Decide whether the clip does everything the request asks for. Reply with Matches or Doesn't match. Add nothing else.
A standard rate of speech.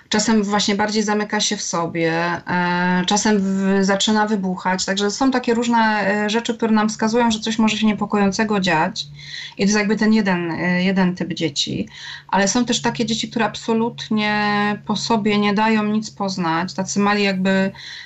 Doesn't match